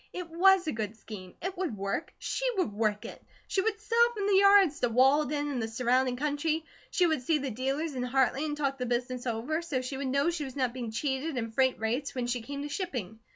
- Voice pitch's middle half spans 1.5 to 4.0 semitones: No, average, 4.7 semitones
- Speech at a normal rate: No, fast, 240 wpm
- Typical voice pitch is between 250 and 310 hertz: Yes, very high, 270 Hz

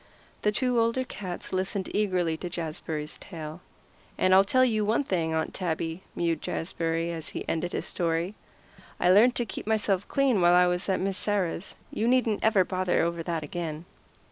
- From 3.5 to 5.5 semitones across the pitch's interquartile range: Yes, average, 4.0 semitones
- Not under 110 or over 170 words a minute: No, average, 180 wpm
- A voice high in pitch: No, medium, 180 Hz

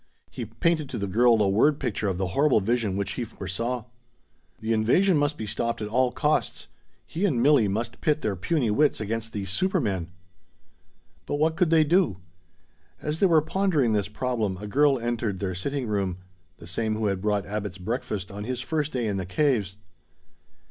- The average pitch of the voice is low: Yes, low, 115 Hz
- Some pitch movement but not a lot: No, wide, 6.2 semitones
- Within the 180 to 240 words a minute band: Yes, average, 190 wpm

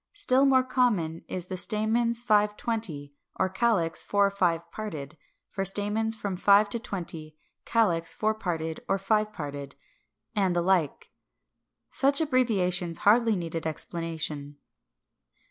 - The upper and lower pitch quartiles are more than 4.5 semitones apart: Yes, average, 4.9 semitones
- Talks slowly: Yes, slow, 130 wpm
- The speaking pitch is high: Yes, high, 195 Hz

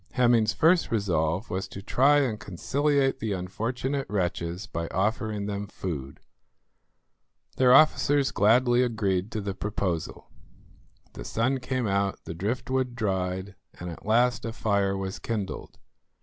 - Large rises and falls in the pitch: No, average, 4.6 semitones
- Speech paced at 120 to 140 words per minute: Yes, slow, 135 wpm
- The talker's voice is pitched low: Yes, low, 105 Hz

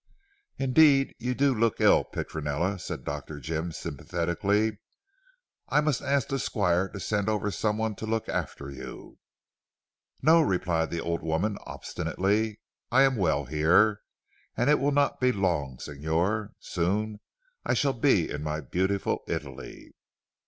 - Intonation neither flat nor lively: No, wide, 5.8 semitones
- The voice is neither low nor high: No, low, 100 Hz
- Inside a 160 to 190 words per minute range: No, average, 145 wpm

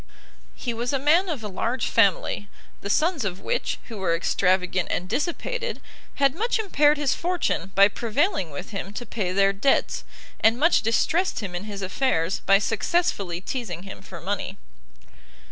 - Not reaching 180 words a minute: Yes, average, 165 wpm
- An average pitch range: No, wide, 7.2 semitones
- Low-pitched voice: No, high, 225 Hz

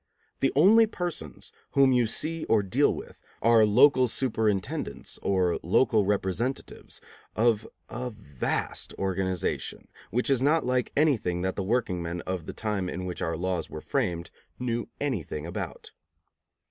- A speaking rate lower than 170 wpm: Yes, average, 140 wpm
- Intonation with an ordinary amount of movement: No, wide, 5.8 semitones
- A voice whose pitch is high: No, low, 110 Hz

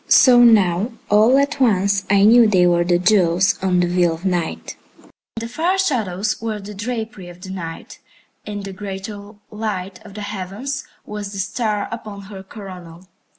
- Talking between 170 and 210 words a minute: Yes, average, 175 wpm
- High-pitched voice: Yes, high, 200 Hz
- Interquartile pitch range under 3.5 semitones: Yes, average, 3.1 semitones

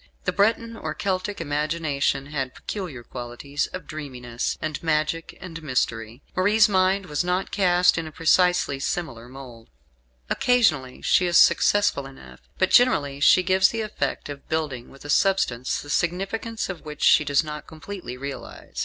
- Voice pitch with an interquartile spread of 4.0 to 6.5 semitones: Yes, wide, 5.4 semitones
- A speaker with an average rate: Yes, average, 155 wpm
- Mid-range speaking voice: Yes, medium, 155 Hz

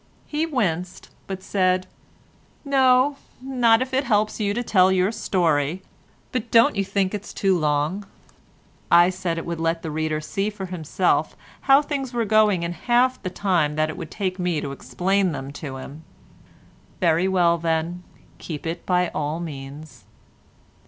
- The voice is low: No, medium, 185 Hz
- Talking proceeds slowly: No, average, 165 wpm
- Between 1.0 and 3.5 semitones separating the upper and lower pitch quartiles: No, average, 4.7 semitones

